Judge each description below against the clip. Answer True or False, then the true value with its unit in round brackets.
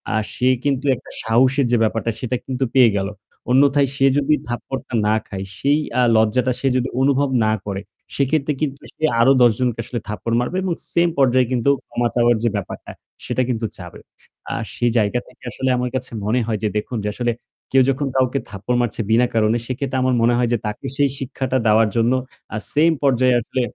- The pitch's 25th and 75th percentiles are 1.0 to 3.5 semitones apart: True (2.7 semitones)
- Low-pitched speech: True (125 Hz)